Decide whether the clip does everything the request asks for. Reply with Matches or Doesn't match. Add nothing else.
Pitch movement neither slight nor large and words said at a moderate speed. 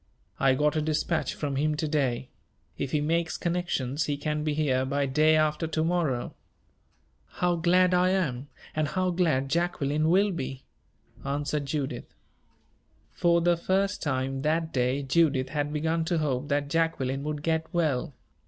Matches